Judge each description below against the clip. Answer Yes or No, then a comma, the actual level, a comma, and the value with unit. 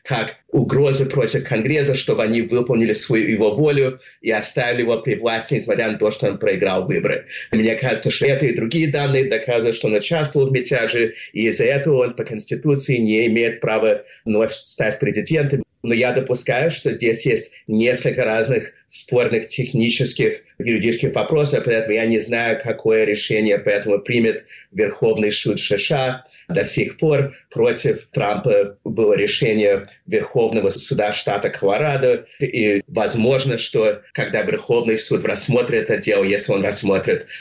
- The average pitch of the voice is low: Yes, low, 130 Hz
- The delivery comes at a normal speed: Yes, average, 150 wpm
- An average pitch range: No, wide, 5.9 semitones